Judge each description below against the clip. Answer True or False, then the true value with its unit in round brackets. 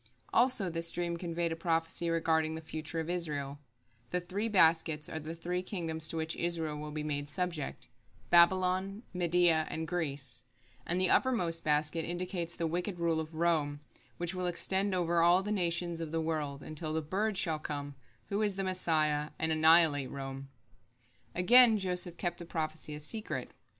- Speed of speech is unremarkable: True (170 wpm)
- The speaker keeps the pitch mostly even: True (2.3 semitones)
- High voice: False (165 Hz)